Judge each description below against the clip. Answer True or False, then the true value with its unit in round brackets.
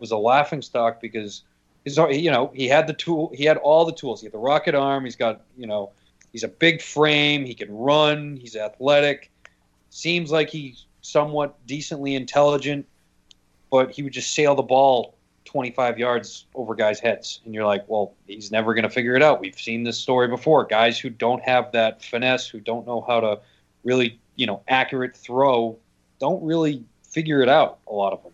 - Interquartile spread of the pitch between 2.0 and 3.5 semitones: False (4.0 semitones)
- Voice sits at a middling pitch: False (125 Hz)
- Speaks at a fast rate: False (195 wpm)